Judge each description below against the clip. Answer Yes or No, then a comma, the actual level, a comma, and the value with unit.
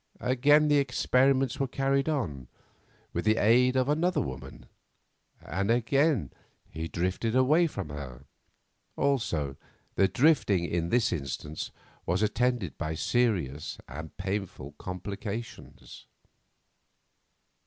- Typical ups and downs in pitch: No, wide, 7.8 semitones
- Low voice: Yes, low, 110 Hz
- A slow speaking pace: Yes, slow, 110 wpm